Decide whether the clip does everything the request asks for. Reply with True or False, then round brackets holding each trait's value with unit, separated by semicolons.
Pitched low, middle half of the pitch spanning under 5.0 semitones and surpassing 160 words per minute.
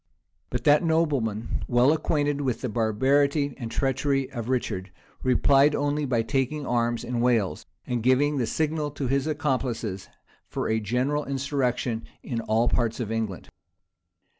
False (130 Hz; 3.7 semitones; 145 wpm)